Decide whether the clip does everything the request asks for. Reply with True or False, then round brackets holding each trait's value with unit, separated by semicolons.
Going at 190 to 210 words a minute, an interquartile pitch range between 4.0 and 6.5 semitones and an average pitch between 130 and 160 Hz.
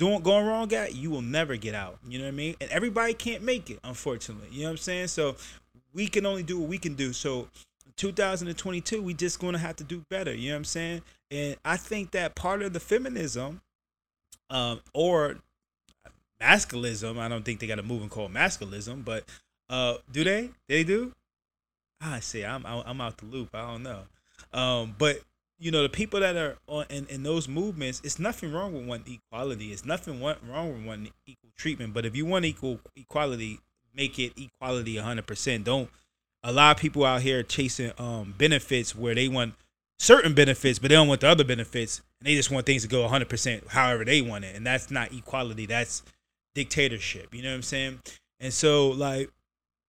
True (205 wpm; 5.2 semitones; 135 Hz)